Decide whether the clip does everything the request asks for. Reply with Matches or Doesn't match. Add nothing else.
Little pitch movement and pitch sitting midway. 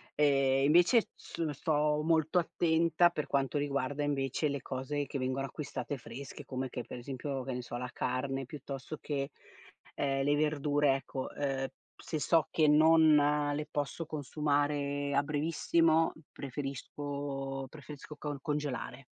Matches